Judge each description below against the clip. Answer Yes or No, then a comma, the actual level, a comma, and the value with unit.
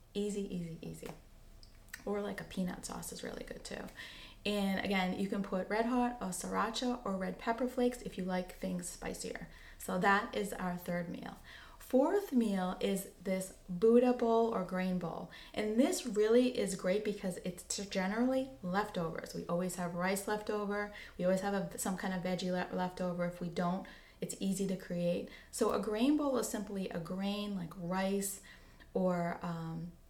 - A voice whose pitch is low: No, high, 195 Hz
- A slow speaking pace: No, average, 175 wpm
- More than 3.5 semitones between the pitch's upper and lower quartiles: No, average, 2.9 semitones